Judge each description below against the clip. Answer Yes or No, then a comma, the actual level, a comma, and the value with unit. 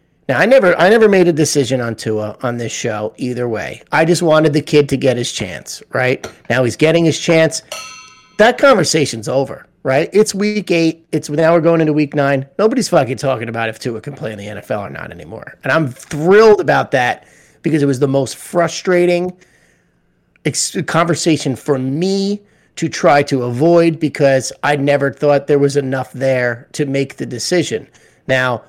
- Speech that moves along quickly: No, average, 185 wpm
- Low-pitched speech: No, medium, 145 Hz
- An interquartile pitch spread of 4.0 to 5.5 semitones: Yes, average, 4.7 semitones